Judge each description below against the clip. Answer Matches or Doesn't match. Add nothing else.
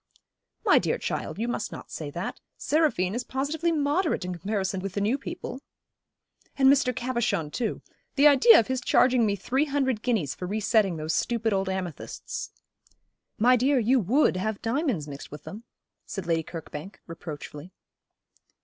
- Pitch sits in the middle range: Doesn't match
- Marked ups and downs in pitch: Matches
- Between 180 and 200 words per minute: Doesn't match